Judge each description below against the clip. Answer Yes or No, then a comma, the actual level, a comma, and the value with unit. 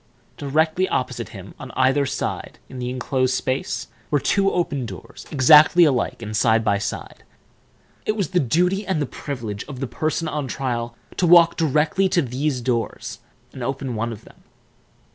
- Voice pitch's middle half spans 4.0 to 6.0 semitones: Yes, average, 4.7 semitones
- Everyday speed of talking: Yes, average, 170 wpm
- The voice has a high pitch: No, low, 135 Hz